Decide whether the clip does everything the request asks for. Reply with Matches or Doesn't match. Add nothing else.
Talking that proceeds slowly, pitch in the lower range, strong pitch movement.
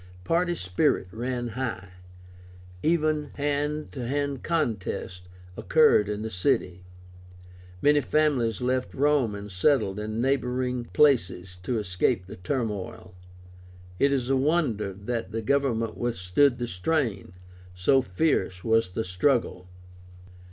Matches